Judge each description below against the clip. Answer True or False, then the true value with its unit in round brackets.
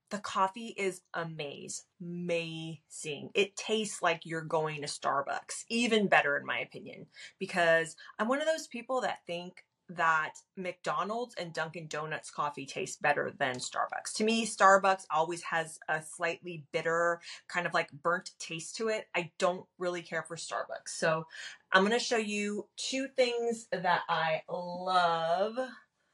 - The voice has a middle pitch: True (175 Hz)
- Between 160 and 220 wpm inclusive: False (150 wpm)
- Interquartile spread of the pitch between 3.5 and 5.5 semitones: True (4.5 semitones)